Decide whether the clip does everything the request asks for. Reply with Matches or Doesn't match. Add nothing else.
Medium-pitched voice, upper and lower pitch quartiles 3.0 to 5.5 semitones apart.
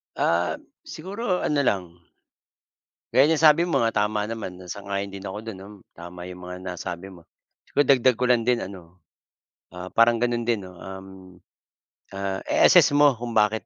Doesn't match